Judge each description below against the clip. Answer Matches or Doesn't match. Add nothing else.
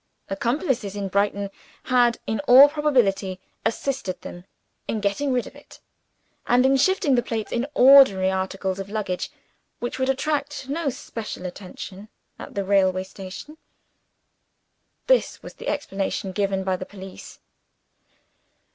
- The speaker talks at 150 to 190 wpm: Doesn't match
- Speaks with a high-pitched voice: Matches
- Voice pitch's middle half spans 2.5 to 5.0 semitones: Doesn't match